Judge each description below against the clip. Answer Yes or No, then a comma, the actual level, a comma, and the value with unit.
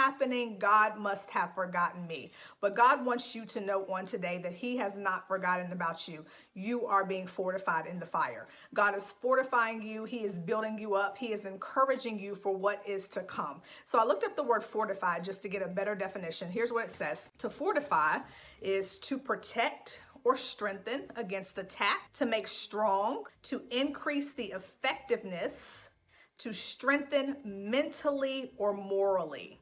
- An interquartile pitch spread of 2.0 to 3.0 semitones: No, average, 4.0 semitones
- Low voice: No, high, 205 Hz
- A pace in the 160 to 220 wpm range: Yes, average, 170 wpm